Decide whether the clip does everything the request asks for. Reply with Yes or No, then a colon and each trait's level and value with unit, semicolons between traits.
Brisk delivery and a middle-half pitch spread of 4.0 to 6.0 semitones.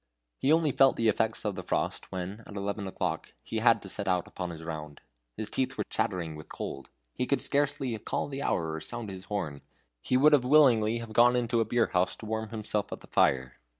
Yes: fast, 215 wpm; average, 5.1 semitones